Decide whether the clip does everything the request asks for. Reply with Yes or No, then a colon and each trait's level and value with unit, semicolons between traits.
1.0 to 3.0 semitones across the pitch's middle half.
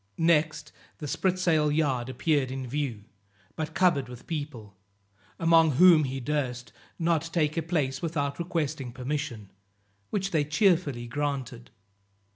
No: average, 3.9 semitones